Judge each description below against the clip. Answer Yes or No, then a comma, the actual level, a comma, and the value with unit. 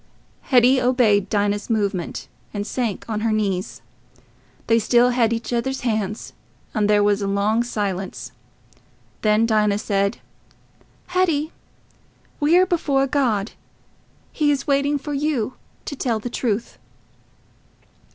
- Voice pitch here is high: Yes, high, 230 Hz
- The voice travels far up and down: No, average, 4.4 semitones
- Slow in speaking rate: Yes, slow, 120 wpm